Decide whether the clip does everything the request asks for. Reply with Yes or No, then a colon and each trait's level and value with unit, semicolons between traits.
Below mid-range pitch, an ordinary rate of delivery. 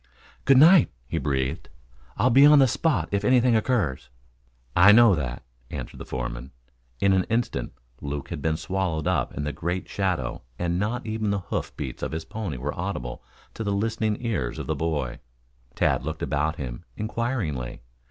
Yes: very low, 95 Hz; average, 175 wpm